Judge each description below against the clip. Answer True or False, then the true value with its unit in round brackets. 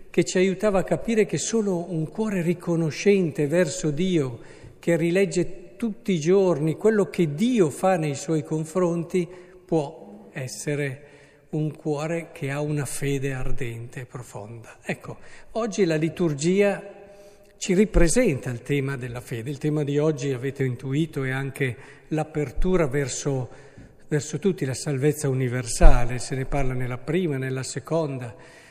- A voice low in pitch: False (155 Hz)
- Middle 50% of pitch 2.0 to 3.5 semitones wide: False (4.7 semitones)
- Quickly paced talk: False (140 wpm)